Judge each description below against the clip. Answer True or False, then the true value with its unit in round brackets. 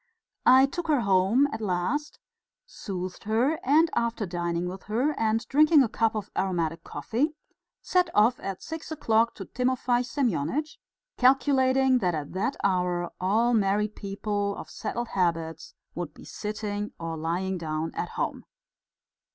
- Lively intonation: True (6.1 semitones)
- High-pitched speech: True (215 Hz)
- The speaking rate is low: False (145 wpm)